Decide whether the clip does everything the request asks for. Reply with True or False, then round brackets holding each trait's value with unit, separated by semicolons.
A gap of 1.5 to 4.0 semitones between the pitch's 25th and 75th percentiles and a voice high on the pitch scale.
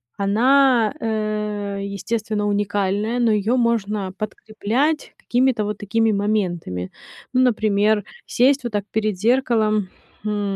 True (2.4 semitones; 215 Hz)